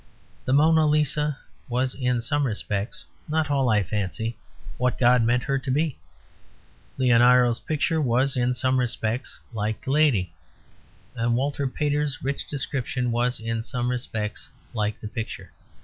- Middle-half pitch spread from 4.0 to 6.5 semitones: No, average, 3.3 semitones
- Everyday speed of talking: Yes, average, 145 wpm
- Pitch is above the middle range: No, low, 125 Hz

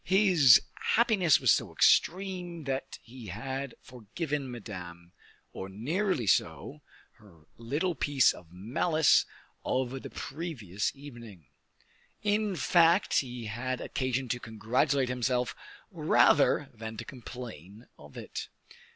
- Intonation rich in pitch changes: Yes, wide, 6.0 semitones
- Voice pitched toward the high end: No, low, 130 Hz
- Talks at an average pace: No, slow, 115 wpm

